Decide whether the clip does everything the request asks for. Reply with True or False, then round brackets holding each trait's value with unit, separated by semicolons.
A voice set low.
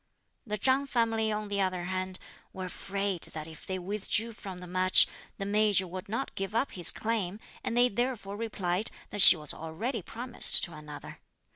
False (200 Hz)